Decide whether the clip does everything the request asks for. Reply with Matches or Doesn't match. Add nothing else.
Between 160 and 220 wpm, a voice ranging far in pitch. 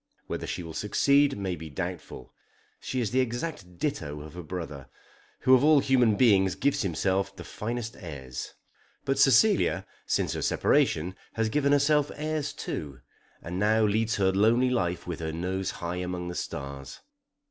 Matches